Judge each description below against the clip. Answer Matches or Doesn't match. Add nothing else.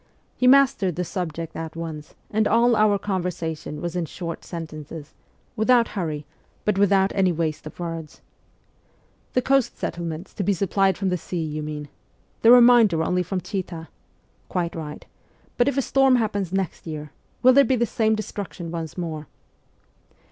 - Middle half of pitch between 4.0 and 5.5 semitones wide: Matches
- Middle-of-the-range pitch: Matches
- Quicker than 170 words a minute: Doesn't match